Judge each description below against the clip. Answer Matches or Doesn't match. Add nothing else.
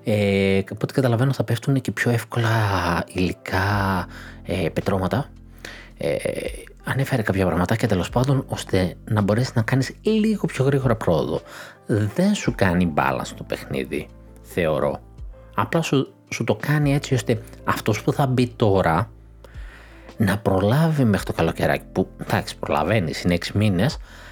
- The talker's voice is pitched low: Matches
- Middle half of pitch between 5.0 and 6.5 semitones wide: Matches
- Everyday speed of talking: Matches